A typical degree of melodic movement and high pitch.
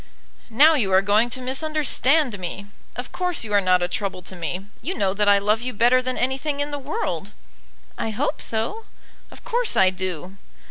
No: wide, 6.5 semitones; high, 225 Hz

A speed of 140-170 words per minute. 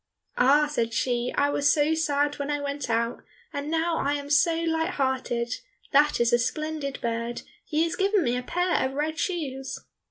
No: average, 190 wpm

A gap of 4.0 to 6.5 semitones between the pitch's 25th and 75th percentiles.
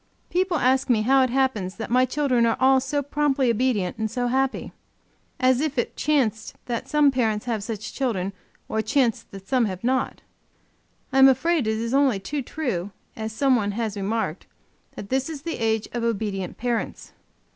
No: average, 3.5 semitones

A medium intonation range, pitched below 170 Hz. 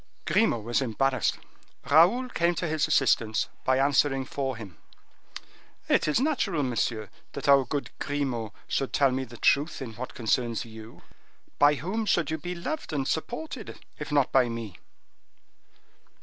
Yes: average, 4.9 semitones; medium, 140 Hz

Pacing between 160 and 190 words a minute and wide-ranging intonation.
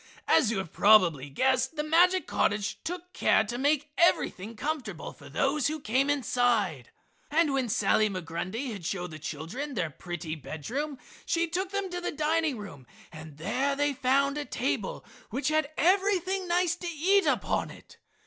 Yes: average, 170 wpm; wide, 8.2 semitones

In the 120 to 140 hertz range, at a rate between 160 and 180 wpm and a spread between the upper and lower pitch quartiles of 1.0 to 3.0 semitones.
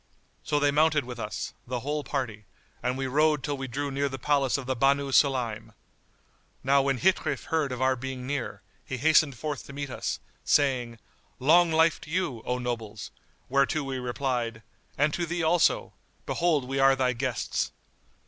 Yes: low, 135 Hz; average, 175 wpm; average, 2.7 semitones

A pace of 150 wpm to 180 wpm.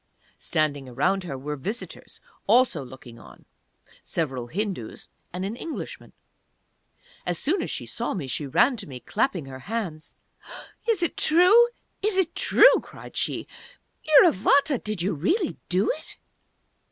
No: average, 140 wpm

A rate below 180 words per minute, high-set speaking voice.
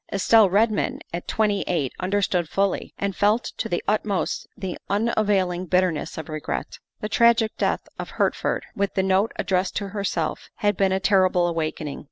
Yes: average, 165 wpm; high, 195 Hz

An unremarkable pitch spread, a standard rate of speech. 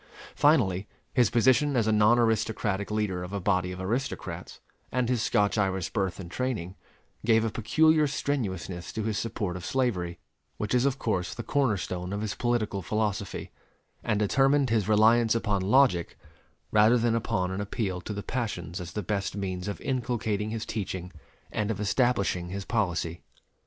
Yes: average, 4.0 semitones; average, 170 wpm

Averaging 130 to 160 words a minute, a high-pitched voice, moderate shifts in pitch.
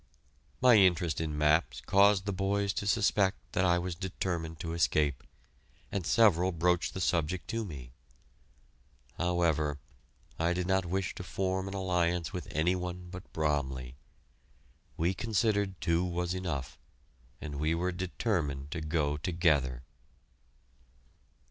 No: slow, 135 wpm; very low, 90 Hz; average, 3.4 semitones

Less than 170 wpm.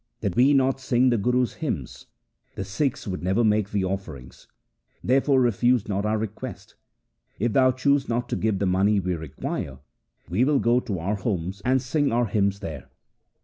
No: average, 180 wpm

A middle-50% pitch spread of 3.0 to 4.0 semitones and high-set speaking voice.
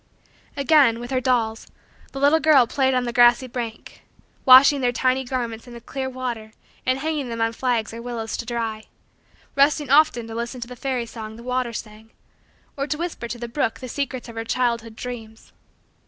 No: narrow, 2.5 semitones; high, 245 Hz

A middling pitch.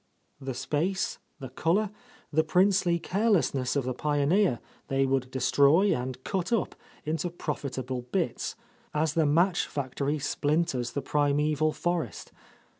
Yes: medium, 150 Hz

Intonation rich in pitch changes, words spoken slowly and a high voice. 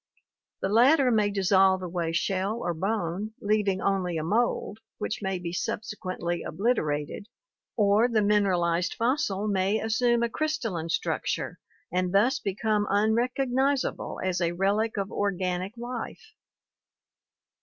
No: average, 3.7 semitones; slow, 125 wpm; high, 205 Hz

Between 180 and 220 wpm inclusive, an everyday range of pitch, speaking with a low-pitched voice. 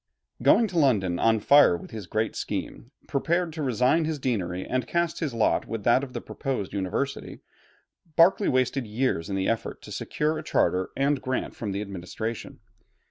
No: average, 185 wpm; wide, 6.1 semitones; low, 125 Hz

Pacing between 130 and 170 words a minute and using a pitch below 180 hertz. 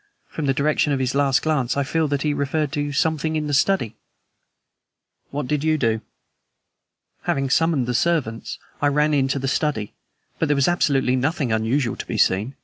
No: average, 185 wpm; medium, 140 Hz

